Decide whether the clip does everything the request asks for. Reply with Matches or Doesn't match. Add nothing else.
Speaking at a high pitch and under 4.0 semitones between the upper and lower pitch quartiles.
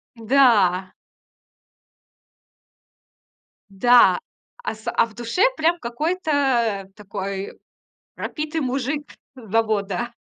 Doesn't match